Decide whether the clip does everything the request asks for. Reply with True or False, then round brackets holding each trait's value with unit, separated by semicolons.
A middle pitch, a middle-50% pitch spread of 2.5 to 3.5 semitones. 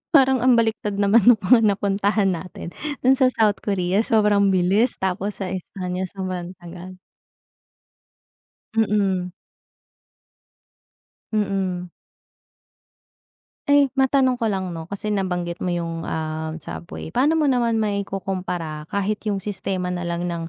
False (195 Hz; 3.2 semitones)